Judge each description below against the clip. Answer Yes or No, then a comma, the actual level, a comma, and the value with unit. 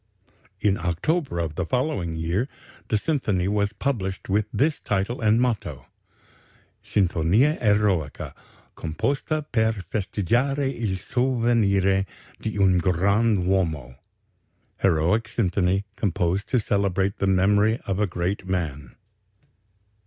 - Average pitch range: Yes, average, 4.1 semitones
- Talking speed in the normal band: No, slow, 110 wpm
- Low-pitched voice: Yes, low, 100 Hz